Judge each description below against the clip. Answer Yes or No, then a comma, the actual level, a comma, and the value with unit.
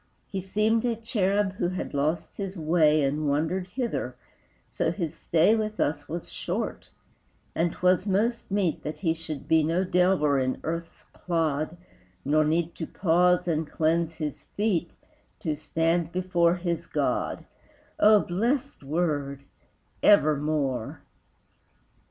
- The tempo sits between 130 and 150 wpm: Yes, slow, 135 wpm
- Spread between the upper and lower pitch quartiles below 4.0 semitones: Yes, average, 3.5 semitones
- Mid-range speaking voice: Yes, medium, 170 Hz